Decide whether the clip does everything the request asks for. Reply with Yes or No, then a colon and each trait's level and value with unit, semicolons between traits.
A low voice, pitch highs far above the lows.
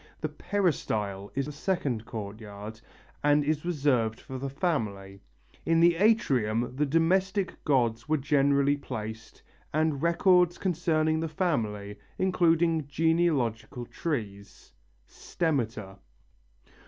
No: medium, 145 Hz; wide, 6.6 semitones